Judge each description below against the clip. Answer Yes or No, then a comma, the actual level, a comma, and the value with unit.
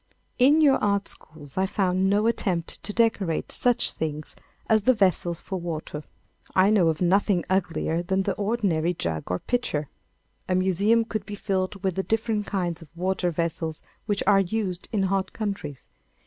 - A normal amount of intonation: Yes, average, 3.5 semitones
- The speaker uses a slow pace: No, average, 170 wpm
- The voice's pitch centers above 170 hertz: Yes, high, 190 Hz